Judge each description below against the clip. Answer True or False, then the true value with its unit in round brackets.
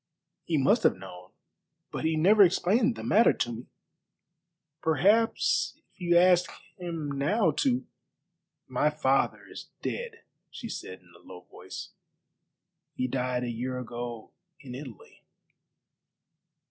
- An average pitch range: False (6.5 semitones)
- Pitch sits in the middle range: True (150 Hz)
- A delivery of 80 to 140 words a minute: True (135 wpm)